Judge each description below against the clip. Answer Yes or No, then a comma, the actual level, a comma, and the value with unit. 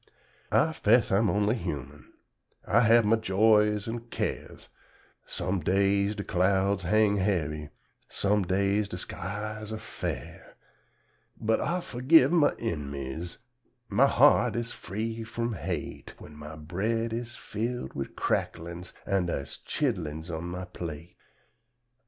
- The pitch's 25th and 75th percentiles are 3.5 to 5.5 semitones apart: Yes, average, 4.4 semitones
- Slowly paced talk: Yes, slow, 130 wpm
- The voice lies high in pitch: No, low, 100 Hz